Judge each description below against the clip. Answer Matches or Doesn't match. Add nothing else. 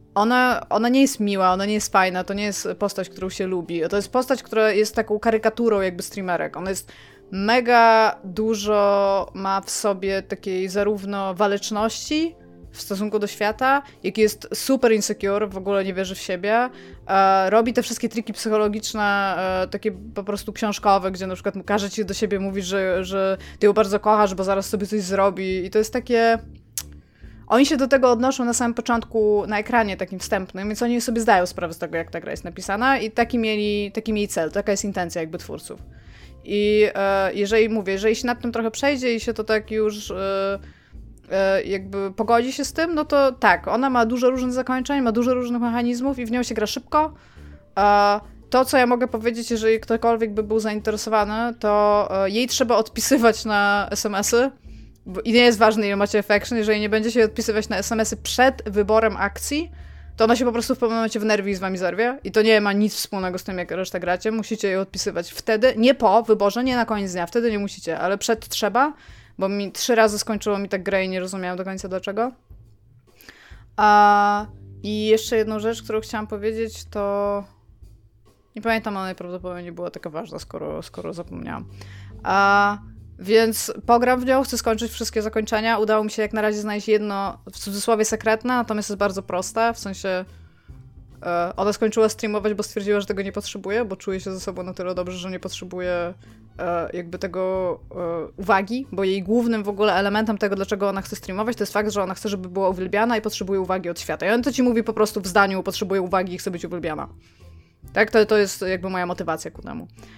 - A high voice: Matches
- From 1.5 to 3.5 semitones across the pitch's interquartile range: Matches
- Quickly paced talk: Matches